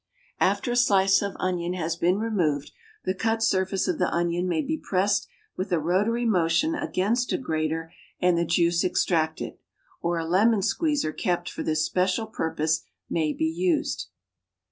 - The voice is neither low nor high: Yes, medium, 180 Hz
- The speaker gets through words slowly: No, average, 165 wpm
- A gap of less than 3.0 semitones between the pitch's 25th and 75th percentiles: No, average, 3.8 semitones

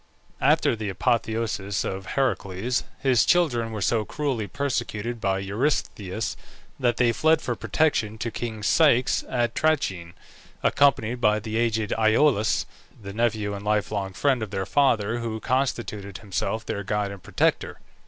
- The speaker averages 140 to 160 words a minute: Yes, average, 145 wpm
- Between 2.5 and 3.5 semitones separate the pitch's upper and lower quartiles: Yes, average, 3.2 semitones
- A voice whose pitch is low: Yes, low, 110 Hz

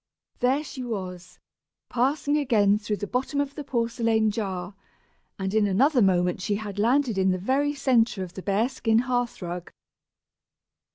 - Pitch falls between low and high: No, high, 225 Hz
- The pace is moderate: Yes, average, 160 wpm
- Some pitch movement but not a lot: Yes, average, 4.9 semitones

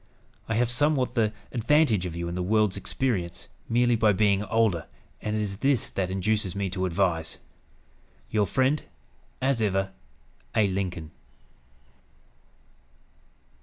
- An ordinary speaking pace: No, slow, 130 wpm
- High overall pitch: No, low, 105 Hz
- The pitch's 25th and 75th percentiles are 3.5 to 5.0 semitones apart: Yes, average, 4.0 semitones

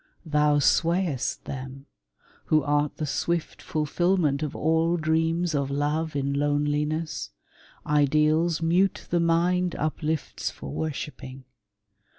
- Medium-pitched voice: Yes, medium, 155 Hz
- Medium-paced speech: No, slow, 115 wpm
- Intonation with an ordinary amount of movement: No, narrow, 2.3 semitones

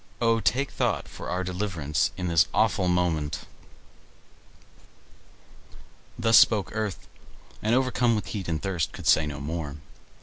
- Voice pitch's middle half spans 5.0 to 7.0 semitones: Yes, wide, 5.5 semitones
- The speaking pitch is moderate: No, very low, 95 Hz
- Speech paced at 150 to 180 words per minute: No, slow, 135 wpm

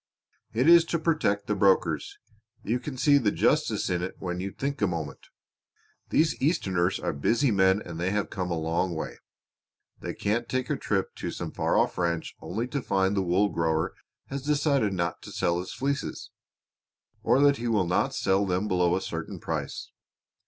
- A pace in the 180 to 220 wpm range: Yes, average, 185 wpm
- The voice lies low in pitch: Yes, low, 100 Hz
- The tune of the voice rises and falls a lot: Yes, wide, 6.6 semitones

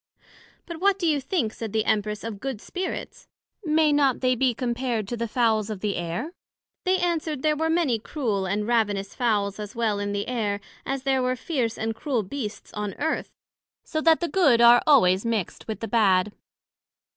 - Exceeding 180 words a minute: Yes, average, 190 wpm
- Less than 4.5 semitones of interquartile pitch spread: No, wide, 5.6 semitones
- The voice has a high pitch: Yes, high, 235 Hz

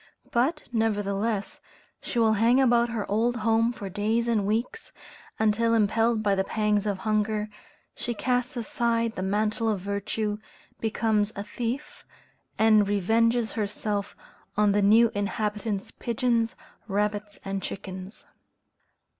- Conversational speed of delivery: No, slow, 130 wpm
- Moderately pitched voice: No, high, 215 Hz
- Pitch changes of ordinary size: No, narrow, 2.0 semitones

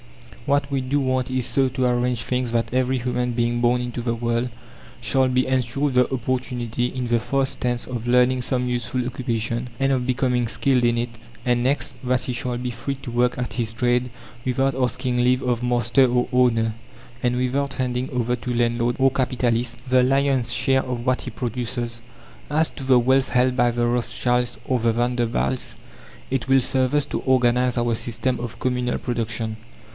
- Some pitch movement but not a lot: No, narrow, 1.3 semitones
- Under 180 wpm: No, average, 185 wpm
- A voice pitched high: No, low, 125 Hz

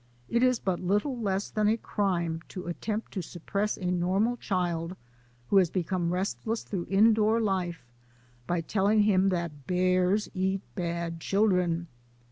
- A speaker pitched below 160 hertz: No, high, 190 Hz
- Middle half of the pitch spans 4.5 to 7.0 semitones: No, average, 3.2 semitones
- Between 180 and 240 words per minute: No, average, 150 wpm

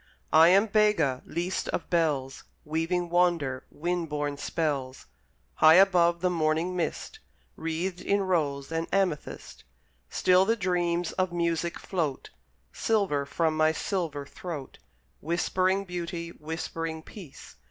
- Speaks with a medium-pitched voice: Yes, medium, 170 Hz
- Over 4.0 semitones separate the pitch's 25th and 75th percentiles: No, average, 2.7 semitones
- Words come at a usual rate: No, slow, 120 wpm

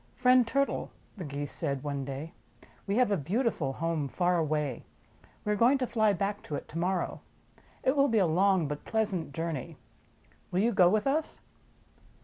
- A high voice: No, medium, 180 Hz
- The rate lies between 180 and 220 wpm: Yes, average, 185 wpm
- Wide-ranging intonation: Yes, wide, 6.5 semitones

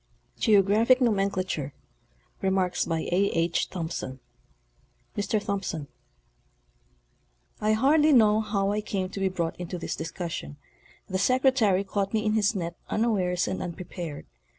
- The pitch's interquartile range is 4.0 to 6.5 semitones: No, average, 3.3 semitones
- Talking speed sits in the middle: No, slow, 115 wpm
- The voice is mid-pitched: No, high, 195 Hz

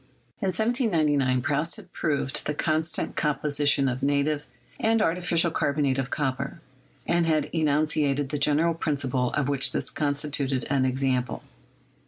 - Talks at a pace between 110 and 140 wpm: Yes, slow, 135 wpm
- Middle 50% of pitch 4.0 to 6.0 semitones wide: No, average, 2.7 semitones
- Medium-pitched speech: Yes, medium, 145 Hz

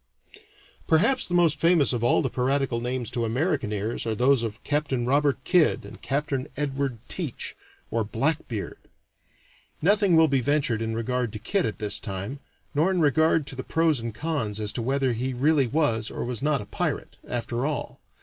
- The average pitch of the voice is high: No, low, 135 Hz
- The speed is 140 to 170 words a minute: No, average, 185 wpm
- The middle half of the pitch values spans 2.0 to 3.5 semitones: No, average, 4.6 semitones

